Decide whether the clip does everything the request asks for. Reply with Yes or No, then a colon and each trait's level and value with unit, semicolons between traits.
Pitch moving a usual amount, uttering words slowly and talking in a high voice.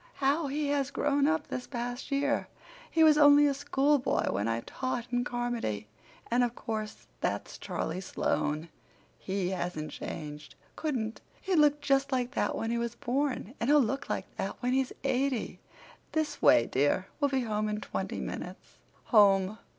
No: average, 5.0 semitones; average, 165 wpm; very high, 250 Hz